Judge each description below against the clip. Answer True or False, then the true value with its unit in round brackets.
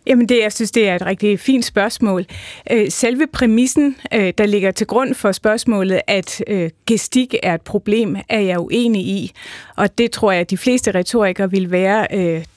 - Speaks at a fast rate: False (175 wpm)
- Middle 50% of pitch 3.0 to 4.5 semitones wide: True (3.5 semitones)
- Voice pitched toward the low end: False (210 Hz)